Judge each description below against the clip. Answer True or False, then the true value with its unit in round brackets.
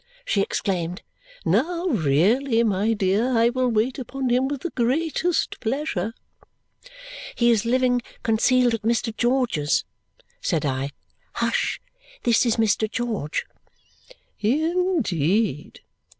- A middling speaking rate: False (115 wpm)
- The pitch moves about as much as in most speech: True (4.2 semitones)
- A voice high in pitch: True (235 Hz)